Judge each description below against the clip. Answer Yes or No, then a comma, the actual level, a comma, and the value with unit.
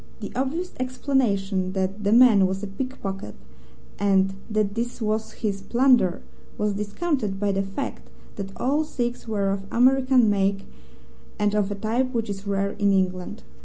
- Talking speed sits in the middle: Yes, average, 160 wpm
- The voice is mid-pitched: No, high, 205 Hz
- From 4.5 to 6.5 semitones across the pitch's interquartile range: No, average, 4.0 semitones